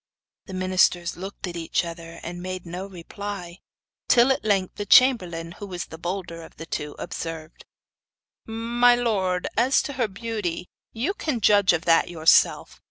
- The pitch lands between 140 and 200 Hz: Yes, medium, 185 Hz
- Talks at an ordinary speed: Yes, average, 165 wpm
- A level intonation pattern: No, average, 4.6 semitones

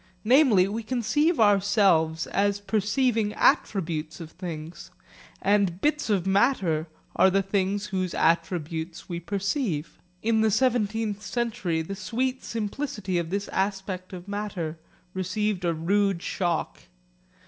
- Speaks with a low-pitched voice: No, high, 195 Hz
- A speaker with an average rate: No, slow, 125 wpm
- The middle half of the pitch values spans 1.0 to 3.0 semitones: No, average, 3.5 semitones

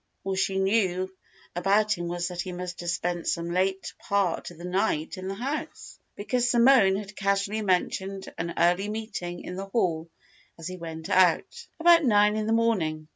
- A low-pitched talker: No, high, 190 Hz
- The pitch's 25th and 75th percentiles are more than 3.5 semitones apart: No, average, 3.1 semitones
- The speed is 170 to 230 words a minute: Yes, average, 180 wpm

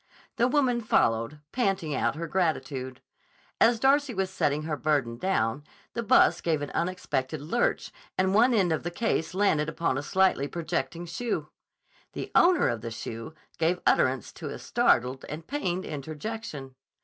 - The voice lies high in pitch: No, medium, 165 Hz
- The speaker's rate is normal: Yes, average, 160 wpm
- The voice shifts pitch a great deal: Yes, wide, 6.1 semitones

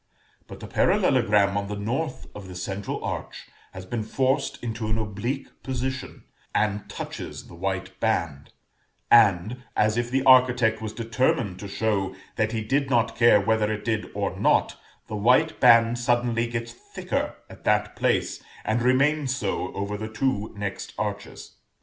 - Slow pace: No, average, 160 wpm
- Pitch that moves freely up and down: No, average, 3.5 semitones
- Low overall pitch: Yes, low, 110 Hz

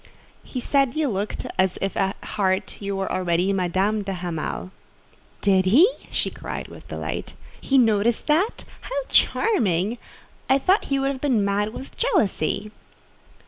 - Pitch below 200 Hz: No, high, 210 Hz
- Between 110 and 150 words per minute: Yes, average, 145 wpm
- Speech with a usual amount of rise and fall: No, wide, 6.2 semitones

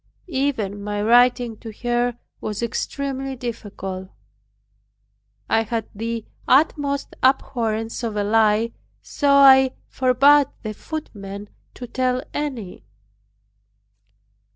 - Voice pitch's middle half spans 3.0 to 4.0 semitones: Yes, average, 3.7 semitones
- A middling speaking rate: No, slow, 100 wpm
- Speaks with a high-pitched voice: Yes, high, 240 Hz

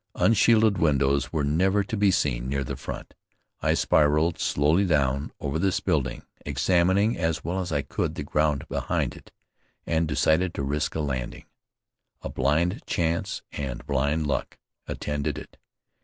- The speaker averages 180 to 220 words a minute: No, average, 155 wpm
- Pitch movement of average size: Yes, average, 4.0 semitones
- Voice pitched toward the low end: Yes, very low, 75 Hz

